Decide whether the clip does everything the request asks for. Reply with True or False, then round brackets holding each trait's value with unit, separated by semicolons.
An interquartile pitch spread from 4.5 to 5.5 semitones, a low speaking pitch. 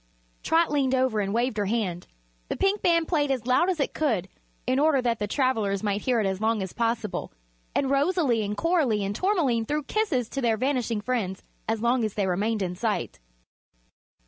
False (5.1 semitones; 235 Hz)